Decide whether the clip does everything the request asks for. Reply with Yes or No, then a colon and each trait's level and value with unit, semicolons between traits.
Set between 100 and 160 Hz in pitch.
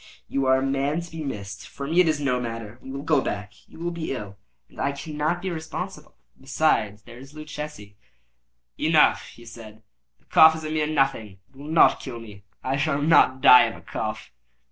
Yes: medium, 140 Hz